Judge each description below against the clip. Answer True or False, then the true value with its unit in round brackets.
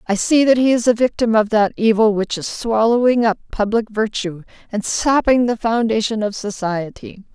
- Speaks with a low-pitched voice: False (220 Hz)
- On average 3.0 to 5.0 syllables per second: True (4.9 syllables/s)